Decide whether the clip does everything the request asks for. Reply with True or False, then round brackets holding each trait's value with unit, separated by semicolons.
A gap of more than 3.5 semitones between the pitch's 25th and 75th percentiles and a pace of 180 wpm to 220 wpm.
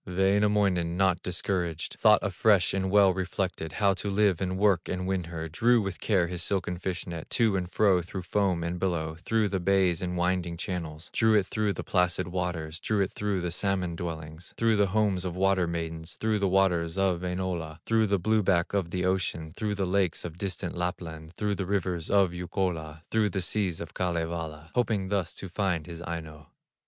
False (2.5 semitones; 195 wpm)